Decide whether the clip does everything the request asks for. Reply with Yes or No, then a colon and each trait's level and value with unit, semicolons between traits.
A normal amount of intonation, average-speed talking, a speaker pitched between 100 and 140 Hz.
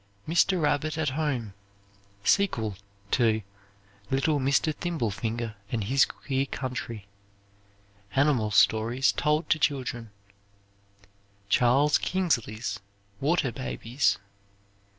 No: average, 4.6 semitones; slow, 90 wpm; low, 135 Hz